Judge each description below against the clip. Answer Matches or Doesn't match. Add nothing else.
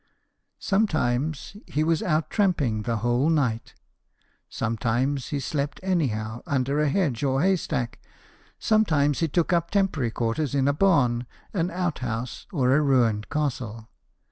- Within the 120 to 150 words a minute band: Matches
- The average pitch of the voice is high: Doesn't match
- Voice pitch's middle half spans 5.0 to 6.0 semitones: Matches